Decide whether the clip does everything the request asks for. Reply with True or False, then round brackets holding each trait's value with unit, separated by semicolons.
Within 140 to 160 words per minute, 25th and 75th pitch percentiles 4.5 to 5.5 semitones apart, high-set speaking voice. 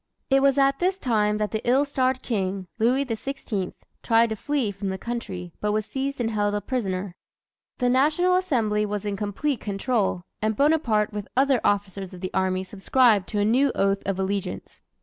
False (190 wpm; 4.9 semitones; 215 Hz)